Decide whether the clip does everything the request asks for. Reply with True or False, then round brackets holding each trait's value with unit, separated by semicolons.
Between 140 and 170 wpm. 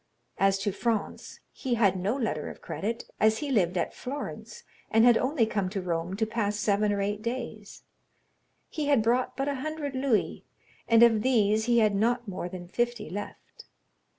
False (180 wpm)